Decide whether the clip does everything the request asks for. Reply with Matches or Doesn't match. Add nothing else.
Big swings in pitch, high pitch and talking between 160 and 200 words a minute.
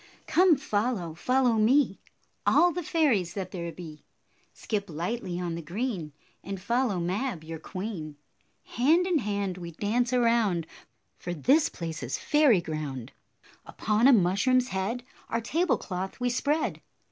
Doesn't match